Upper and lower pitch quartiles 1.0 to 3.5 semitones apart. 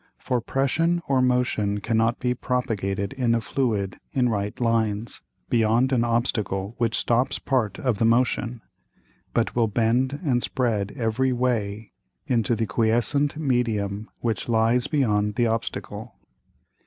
Yes: narrow, 2.5 semitones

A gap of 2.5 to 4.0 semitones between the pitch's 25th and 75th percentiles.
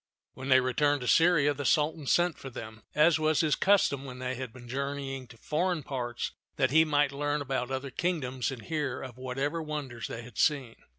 Yes: average, 2.9 semitones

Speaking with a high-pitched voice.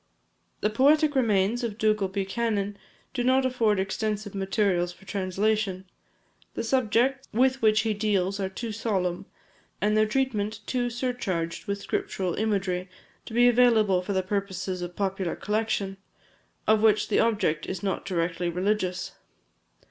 Yes: high, 210 Hz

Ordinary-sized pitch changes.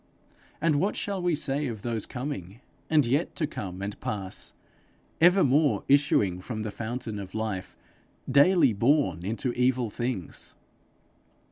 No: wide, 5.8 semitones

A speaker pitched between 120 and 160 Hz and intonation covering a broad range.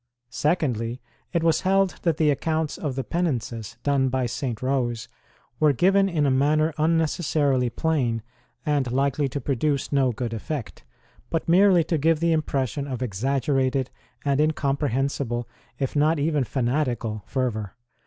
No: medium, 140 Hz; average, 3.8 semitones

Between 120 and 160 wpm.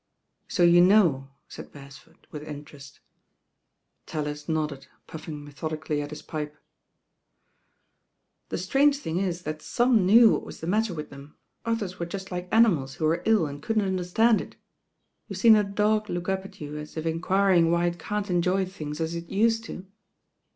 No: average, 170 wpm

